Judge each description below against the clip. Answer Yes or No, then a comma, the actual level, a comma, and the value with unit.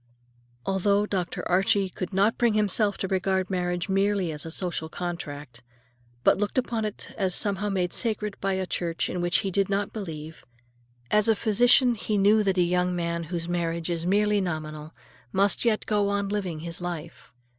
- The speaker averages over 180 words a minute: No, average, 175 wpm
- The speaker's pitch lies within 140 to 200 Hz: Yes, high, 190 Hz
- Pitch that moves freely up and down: No, average, 3.2 semitones